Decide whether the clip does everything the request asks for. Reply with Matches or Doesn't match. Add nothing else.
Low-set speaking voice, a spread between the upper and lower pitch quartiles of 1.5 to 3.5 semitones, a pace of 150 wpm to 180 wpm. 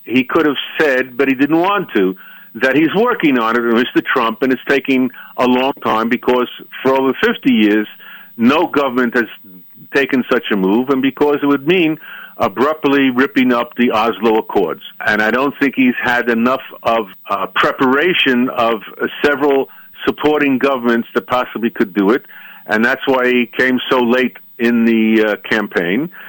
Matches